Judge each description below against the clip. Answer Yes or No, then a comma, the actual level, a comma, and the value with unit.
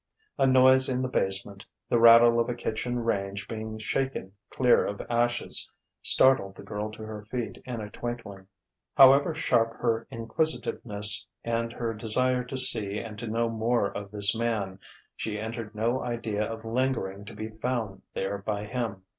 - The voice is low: Yes, low, 115 Hz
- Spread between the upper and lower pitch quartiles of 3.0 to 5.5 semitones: No, narrow, 2.6 semitones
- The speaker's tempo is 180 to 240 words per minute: No, average, 165 wpm